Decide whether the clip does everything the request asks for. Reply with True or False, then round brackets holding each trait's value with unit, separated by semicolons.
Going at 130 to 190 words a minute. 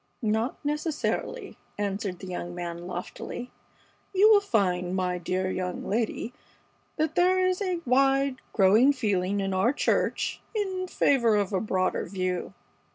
True (140 wpm)